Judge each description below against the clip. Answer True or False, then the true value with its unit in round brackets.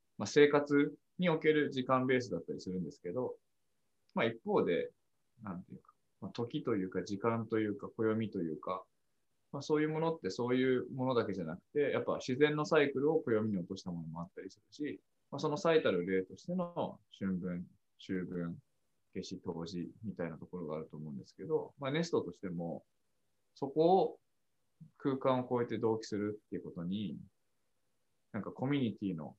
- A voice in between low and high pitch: False (120 Hz)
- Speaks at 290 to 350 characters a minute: False (365 characters per minute)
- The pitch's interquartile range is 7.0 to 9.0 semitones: True (7.9 semitones)